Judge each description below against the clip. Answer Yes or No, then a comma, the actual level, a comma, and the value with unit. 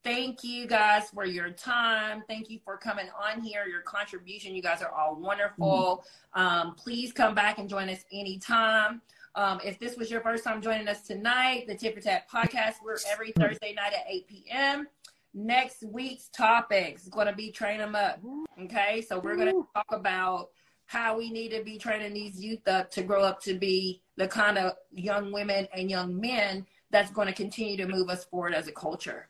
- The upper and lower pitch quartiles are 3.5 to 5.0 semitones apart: No, average, 2.8 semitones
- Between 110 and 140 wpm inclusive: No, average, 200 wpm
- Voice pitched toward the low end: No, high, 205 Hz